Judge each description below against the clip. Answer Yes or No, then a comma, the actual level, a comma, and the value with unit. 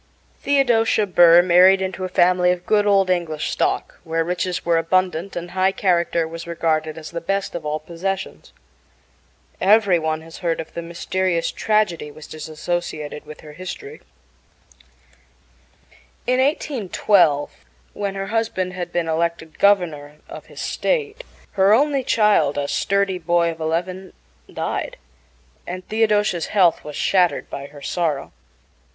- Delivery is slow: No, average, 145 wpm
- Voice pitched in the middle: Yes, medium, 175 Hz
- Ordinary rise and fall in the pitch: Yes, average, 3.0 semitones